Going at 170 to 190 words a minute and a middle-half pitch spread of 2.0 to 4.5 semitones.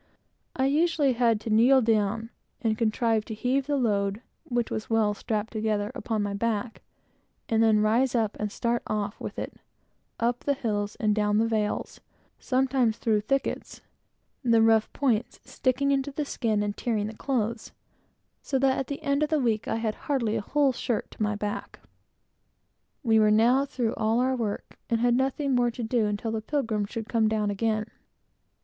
Yes: average, 180 wpm; average, 3.1 semitones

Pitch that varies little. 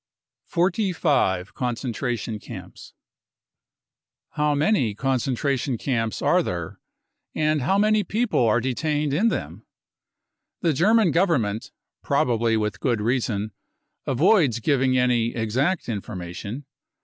No: wide, 5.5 semitones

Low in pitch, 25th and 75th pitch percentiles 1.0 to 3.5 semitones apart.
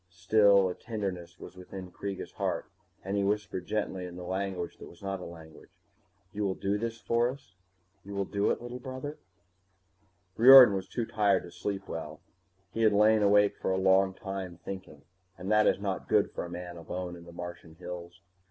Yes: very low, 95 Hz; average, 2.7 semitones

